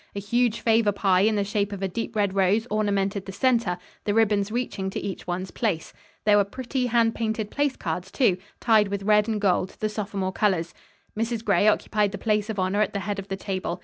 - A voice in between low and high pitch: No, high, 205 Hz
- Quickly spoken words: Yes, fast, 220 wpm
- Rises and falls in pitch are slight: Yes, narrow, 2.3 semitones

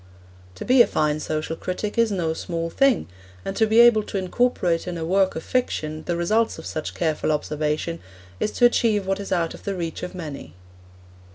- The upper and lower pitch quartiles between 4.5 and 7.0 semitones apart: Yes, average, 5.0 semitones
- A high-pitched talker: No, medium, 180 Hz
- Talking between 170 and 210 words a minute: Yes, average, 200 wpm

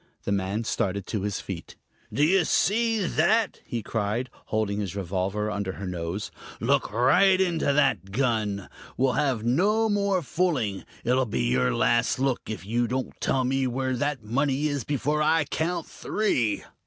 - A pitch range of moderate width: No, wide, 6.8 semitones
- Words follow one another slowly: No, average, 165 wpm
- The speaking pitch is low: Yes, low, 125 Hz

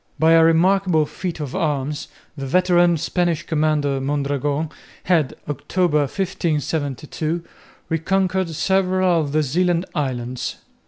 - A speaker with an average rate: No, slow, 110 wpm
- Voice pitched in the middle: Yes, medium, 160 Hz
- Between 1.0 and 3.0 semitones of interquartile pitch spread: No, average, 3.5 semitones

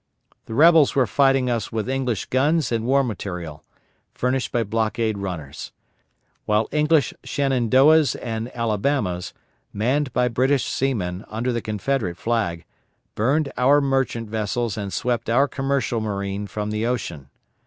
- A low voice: Yes, low, 120 Hz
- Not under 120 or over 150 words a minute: Yes, slow, 135 wpm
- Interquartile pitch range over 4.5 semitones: No, average, 4.2 semitones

